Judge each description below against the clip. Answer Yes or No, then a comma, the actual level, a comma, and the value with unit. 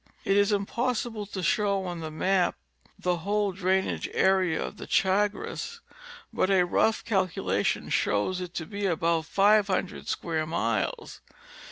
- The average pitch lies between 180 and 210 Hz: Yes, high, 190 Hz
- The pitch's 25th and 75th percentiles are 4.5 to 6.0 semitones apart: No, average, 2.8 semitones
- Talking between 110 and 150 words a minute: Yes, average, 145 wpm